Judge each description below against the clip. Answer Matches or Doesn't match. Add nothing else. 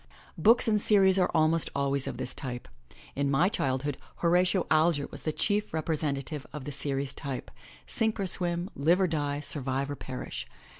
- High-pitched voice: Doesn't match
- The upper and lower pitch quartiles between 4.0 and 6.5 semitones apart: Matches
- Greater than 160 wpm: Matches